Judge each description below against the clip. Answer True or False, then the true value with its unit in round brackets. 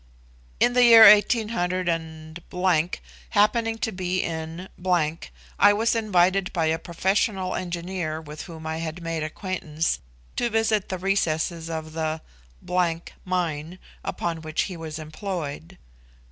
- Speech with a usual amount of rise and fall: True (3.2 semitones)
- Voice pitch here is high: False (175 Hz)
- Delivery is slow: True (130 wpm)